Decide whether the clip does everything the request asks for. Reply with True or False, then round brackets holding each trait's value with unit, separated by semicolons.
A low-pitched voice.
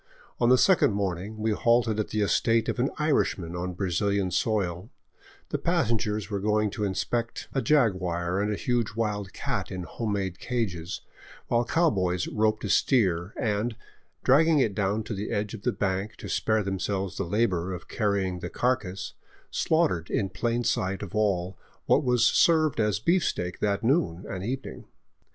True (105 Hz)